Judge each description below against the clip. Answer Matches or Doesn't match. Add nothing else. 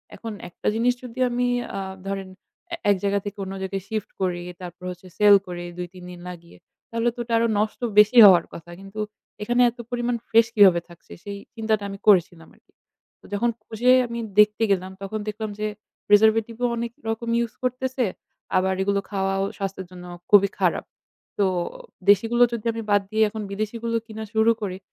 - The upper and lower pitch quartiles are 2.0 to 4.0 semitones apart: Matches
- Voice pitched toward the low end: Doesn't match